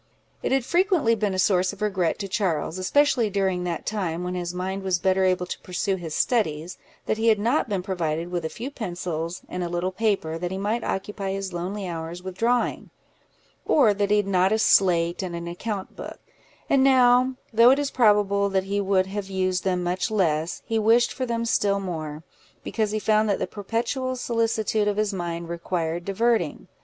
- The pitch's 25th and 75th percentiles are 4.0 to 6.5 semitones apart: No, average, 3.6 semitones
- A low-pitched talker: No, high, 195 Hz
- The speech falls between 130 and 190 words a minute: No, average, 200 wpm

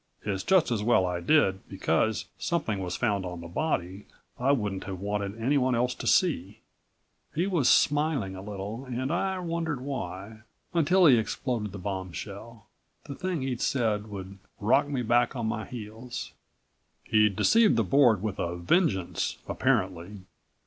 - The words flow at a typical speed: Yes, average, 155 wpm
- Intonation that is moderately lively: No, wide, 6.0 semitones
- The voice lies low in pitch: Yes, low, 110 Hz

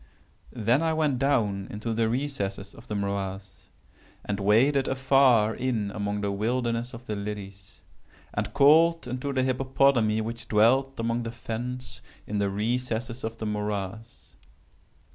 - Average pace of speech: Yes, average, 145 wpm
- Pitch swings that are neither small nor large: Yes, average, 3.8 semitones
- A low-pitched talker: Yes, low, 115 Hz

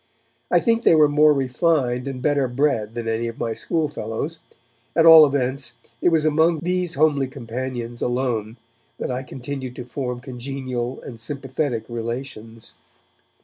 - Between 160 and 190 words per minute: No, average, 145 wpm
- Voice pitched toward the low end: Yes, low, 130 Hz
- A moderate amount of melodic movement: Yes, average, 3.8 semitones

